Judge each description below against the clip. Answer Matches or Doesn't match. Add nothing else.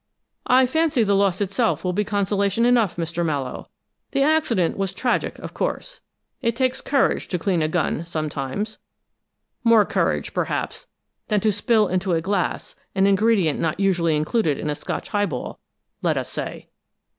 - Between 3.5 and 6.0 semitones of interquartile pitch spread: Matches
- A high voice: Matches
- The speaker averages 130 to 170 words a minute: Matches